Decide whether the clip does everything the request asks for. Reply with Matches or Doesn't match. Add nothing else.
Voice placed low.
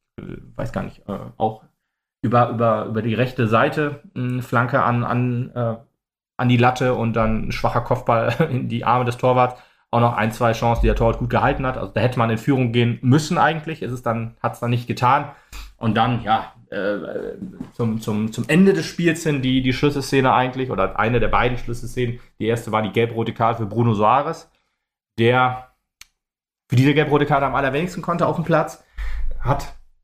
Matches